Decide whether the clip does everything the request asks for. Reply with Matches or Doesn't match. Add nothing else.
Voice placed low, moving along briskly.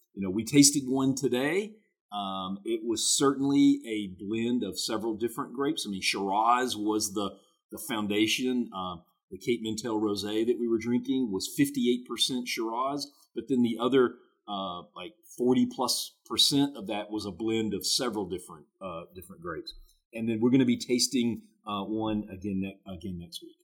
Doesn't match